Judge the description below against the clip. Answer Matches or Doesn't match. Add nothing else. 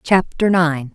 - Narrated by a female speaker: Matches